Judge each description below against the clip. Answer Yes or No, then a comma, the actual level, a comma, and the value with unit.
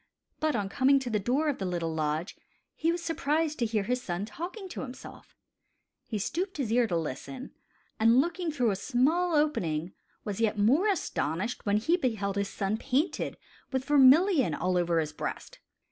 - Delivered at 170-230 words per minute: Yes, average, 180 wpm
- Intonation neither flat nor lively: No, wide, 7.5 semitones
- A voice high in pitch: Yes, high, 245 Hz